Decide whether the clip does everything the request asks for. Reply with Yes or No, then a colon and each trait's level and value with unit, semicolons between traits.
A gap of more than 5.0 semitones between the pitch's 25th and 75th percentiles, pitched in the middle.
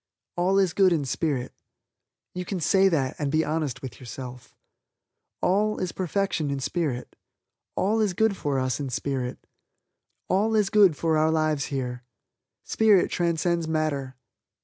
Yes: wide, 5.6 semitones; medium, 160 Hz